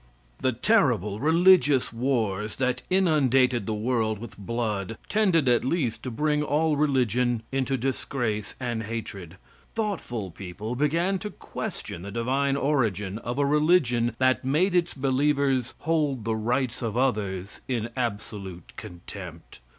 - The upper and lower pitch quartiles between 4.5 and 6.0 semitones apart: Yes, average, 4.8 semitones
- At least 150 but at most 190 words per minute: No, slow, 135 wpm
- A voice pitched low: Yes, low, 125 Hz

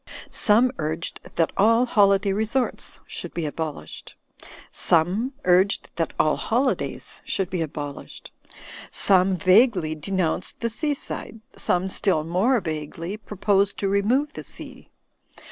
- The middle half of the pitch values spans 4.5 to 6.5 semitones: Yes, average, 4.8 semitones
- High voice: Yes, high, 195 Hz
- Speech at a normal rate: No, slow, 130 wpm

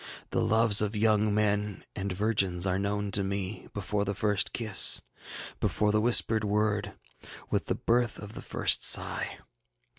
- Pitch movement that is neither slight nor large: No, narrow, 1.3 semitones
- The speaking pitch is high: No, low, 105 Hz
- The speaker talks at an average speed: Yes, average, 155 wpm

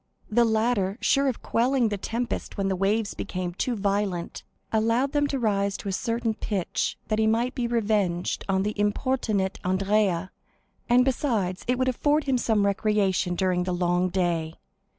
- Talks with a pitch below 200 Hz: No, high, 210 Hz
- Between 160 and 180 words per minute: Yes, average, 170 wpm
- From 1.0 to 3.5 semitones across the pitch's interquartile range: No, average, 4.0 semitones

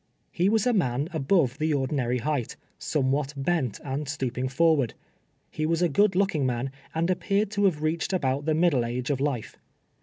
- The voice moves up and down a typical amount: Yes, average, 4.4 semitones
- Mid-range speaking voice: Yes, medium, 150 Hz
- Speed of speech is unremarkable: Yes, average, 185 wpm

